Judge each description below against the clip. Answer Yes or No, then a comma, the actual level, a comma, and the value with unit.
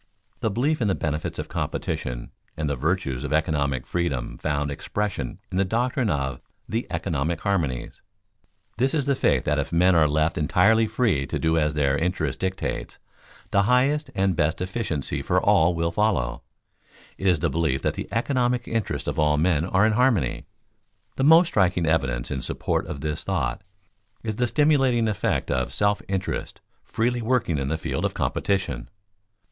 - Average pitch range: No, wide, 7.0 semitones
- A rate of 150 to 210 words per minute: Yes, average, 175 wpm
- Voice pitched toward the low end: Yes, very low, 90 Hz